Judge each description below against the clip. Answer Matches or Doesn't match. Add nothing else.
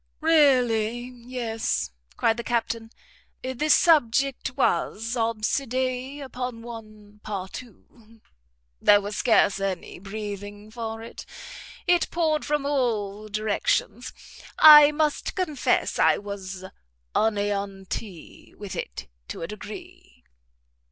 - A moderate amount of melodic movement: Matches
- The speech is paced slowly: Matches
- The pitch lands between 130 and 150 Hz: Doesn't match